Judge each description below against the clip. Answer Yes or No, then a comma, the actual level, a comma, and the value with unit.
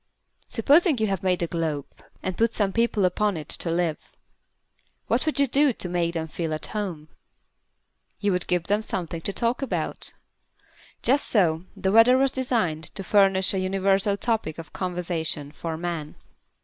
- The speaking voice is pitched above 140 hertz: Yes, high, 190 Hz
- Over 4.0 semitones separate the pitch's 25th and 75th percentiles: Yes, average, 4.8 semitones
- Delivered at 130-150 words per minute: No, average, 170 wpm